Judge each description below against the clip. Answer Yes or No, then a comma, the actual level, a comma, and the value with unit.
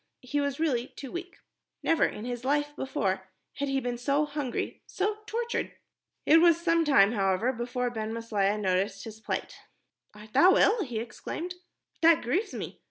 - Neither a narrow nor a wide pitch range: No, wide, 6.6 semitones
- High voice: Yes, very high, 260 Hz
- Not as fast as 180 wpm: Yes, average, 165 wpm